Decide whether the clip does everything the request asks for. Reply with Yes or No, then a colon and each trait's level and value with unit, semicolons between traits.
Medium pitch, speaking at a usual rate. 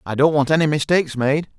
No: medium, 145 Hz; fast, 225 wpm